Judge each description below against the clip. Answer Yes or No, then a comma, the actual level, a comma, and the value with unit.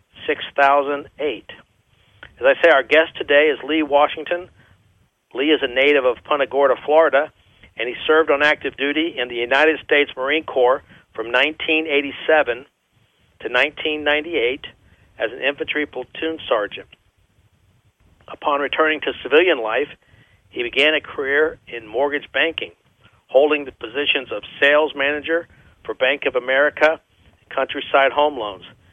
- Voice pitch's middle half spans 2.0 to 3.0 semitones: Yes, average, 2.7 semitones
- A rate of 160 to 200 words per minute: No, slow, 135 wpm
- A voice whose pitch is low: No, medium, 145 Hz